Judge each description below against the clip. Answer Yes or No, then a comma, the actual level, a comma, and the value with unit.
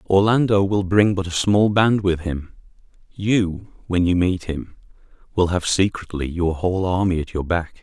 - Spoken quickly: No, average, 175 wpm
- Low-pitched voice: Yes, very low, 90 Hz